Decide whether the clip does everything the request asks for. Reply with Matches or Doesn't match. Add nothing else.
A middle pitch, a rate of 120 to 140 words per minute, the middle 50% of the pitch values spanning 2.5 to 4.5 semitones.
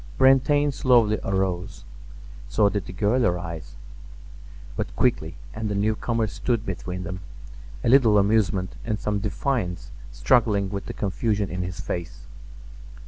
Doesn't match